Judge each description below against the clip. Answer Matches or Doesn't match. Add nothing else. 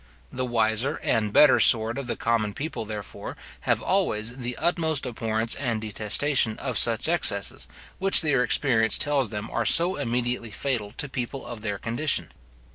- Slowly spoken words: Doesn't match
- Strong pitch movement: Doesn't match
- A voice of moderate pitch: Doesn't match